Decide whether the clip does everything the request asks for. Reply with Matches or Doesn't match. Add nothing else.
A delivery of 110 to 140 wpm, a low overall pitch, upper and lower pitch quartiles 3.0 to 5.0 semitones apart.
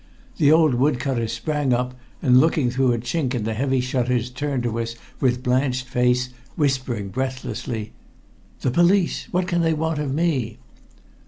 Doesn't match